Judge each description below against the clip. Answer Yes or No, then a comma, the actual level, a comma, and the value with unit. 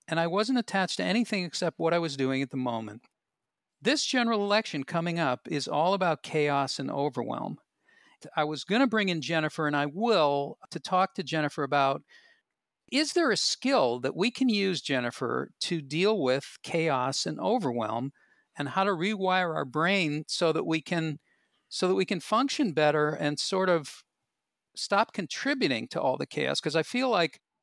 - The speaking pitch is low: No, medium, 165 Hz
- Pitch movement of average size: No, wide, 5.7 semitones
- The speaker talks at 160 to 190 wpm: Yes, average, 180 wpm